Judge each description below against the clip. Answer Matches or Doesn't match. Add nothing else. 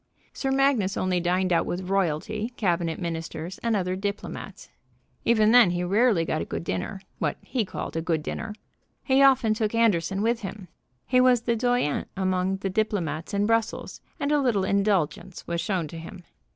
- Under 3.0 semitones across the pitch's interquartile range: Doesn't match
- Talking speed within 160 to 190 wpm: Matches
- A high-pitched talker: Matches